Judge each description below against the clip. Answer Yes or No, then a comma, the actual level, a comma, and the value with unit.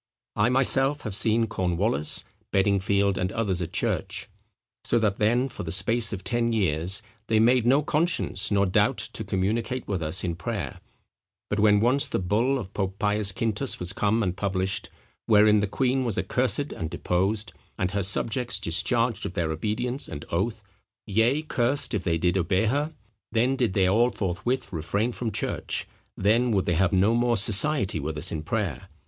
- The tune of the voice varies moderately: Yes, average, 4.2 semitones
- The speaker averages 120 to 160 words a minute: No, average, 175 wpm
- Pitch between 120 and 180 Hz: No, low, 105 Hz